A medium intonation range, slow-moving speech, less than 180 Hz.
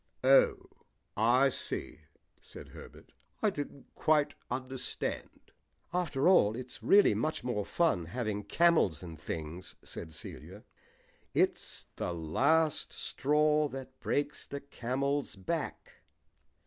No: wide, 6.8 semitones; slow, 110 wpm; low, 135 Hz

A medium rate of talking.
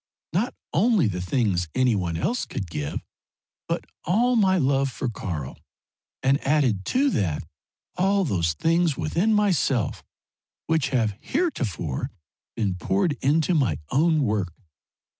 No: slow, 130 wpm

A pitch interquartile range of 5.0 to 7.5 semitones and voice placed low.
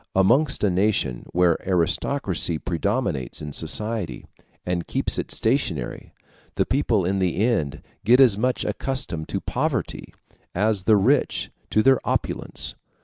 Yes: wide, 5.5 semitones; low, 100 Hz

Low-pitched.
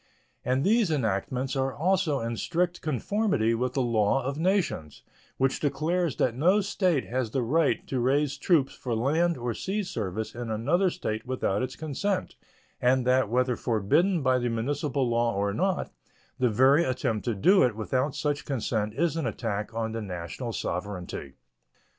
Yes: low, 130 Hz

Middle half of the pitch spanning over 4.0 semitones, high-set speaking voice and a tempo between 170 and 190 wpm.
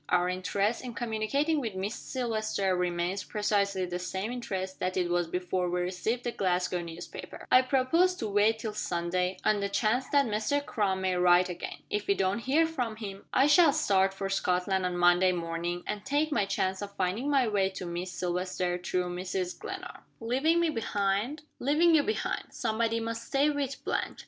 Yes: average, 5.1 semitones; high, 200 Hz; average, 185 wpm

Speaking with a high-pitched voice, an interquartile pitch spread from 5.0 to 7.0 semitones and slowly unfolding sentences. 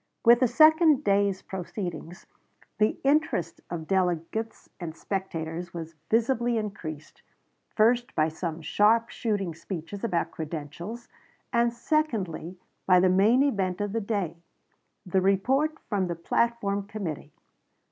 Yes: high, 200 Hz; average, 5.3 semitones; slow, 125 wpm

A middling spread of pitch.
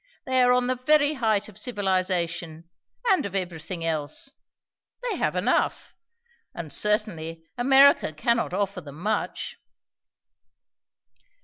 No: wide, 6.9 semitones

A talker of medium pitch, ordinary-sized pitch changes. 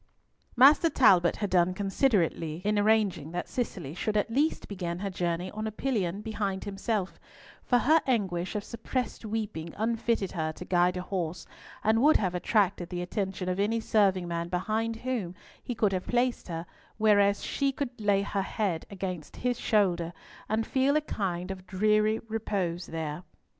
No: high, 200 Hz; average, 3.8 semitones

